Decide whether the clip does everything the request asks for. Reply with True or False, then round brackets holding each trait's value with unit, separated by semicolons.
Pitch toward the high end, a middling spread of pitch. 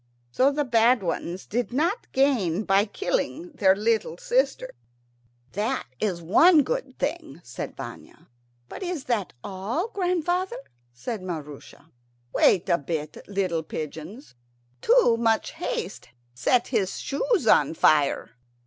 False (225 Hz; 9.0 semitones)